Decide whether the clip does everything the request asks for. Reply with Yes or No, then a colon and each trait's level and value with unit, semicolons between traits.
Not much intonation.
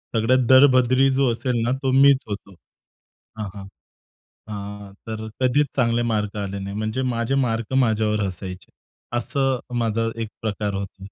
No: average, 3.9 semitones